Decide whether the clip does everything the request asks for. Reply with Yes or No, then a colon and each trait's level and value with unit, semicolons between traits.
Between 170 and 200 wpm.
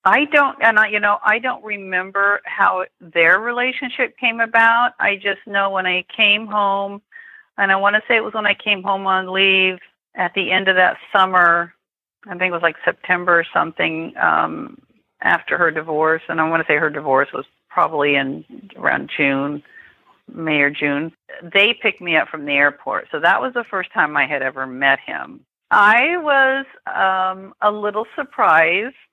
Yes: average, 185 wpm